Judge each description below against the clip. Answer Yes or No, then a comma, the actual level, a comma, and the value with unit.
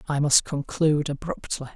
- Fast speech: No, slow, 135 wpm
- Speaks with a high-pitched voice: No, medium, 150 Hz